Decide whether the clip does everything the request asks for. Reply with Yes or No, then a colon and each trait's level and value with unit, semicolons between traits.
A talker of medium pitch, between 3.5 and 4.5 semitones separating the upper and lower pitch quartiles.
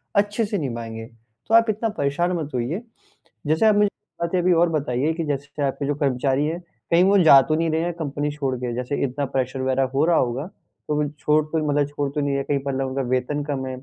Yes: medium, 145 Hz; average, 3.8 semitones